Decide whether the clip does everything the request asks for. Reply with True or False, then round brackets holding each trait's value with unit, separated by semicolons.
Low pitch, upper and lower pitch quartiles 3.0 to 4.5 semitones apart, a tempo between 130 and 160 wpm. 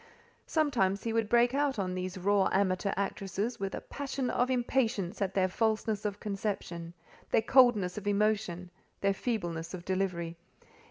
False (200 Hz; 3.6 semitones; 155 wpm)